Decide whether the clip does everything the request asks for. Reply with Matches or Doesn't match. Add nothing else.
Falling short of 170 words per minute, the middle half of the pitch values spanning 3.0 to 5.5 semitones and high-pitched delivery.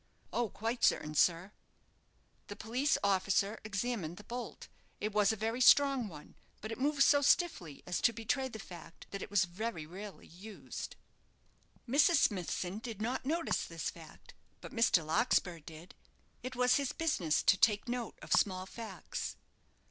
Matches